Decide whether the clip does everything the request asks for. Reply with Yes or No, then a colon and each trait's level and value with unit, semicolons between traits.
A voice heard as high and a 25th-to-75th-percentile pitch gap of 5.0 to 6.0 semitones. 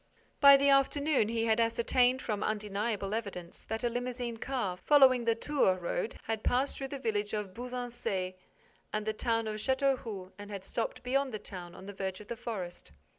No: high, 225 Hz; average, 3.7 semitones